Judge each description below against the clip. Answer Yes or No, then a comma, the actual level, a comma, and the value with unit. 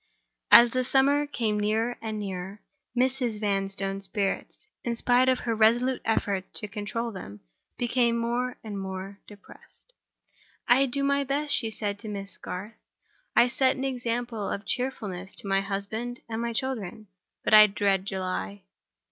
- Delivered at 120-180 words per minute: Yes, average, 150 wpm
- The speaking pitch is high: Yes, high, 220 Hz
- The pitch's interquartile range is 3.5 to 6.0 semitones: Yes, average, 3.8 semitones